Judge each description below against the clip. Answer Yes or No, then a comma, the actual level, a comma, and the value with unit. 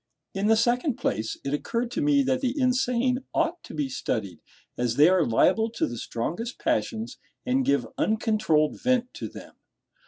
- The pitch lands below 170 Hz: No, high, 230 Hz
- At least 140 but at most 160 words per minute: No, average, 175 wpm